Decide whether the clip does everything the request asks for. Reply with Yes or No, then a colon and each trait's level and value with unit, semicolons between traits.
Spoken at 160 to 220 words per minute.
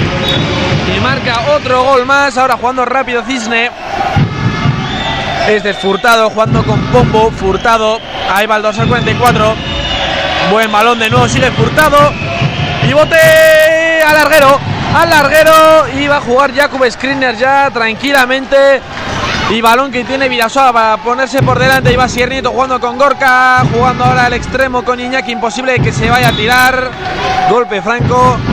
No: average, 150 wpm